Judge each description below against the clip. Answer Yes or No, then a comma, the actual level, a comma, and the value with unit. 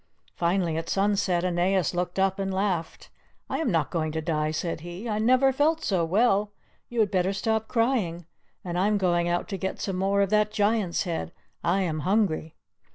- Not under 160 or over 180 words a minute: No, average, 195 wpm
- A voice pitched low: No, high, 190 Hz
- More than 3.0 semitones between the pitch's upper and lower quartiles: Yes, average, 3.4 semitones